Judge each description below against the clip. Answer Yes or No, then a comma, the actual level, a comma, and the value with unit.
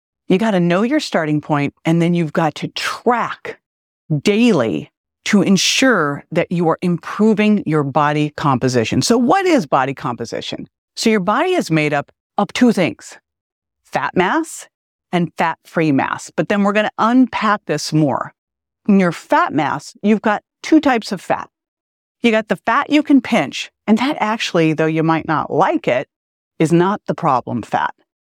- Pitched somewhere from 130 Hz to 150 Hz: No, high, 190 Hz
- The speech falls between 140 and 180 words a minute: Yes, average, 175 wpm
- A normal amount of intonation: No, wide, 5.8 semitones